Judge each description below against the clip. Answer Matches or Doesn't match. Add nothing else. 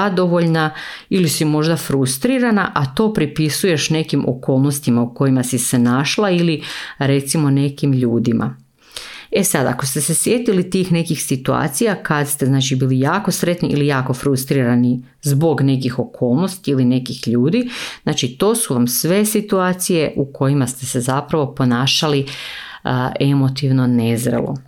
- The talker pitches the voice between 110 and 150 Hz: Matches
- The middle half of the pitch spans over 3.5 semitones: Matches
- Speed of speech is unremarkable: Matches